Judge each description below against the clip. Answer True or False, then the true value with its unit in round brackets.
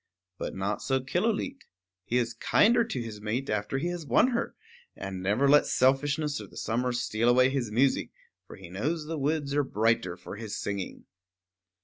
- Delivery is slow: False (190 wpm)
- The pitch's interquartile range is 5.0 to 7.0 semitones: True (5.5 semitones)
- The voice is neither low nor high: False (130 Hz)